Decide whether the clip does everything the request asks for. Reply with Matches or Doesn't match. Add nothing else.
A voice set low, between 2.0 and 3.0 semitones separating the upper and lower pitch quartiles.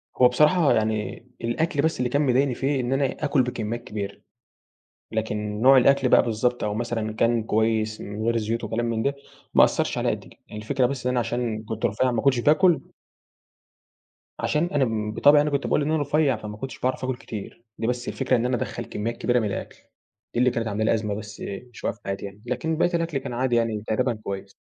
Doesn't match